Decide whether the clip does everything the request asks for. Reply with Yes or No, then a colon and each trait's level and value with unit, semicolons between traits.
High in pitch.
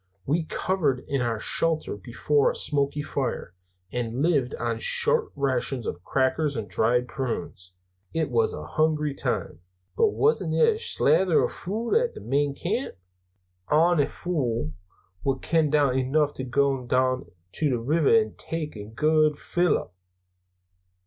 No: medium, 140 Hz